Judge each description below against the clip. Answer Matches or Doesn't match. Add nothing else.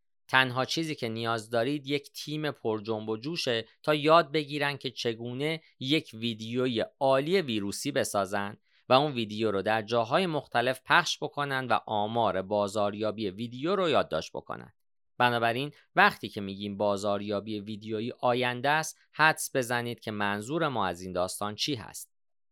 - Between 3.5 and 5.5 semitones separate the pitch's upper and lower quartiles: Matches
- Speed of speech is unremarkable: Matches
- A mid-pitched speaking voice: Doesn't match